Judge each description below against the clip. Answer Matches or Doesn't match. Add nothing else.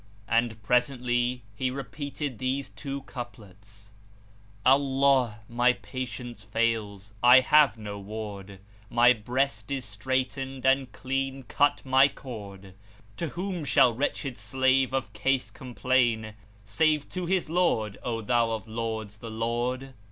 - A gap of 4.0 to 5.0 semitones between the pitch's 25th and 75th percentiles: Doesn't match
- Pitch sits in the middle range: Doesn't match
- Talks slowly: Matches